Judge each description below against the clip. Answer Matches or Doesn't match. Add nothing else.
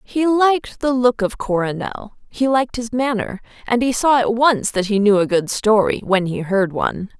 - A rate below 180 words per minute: Doesn't match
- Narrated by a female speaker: Matches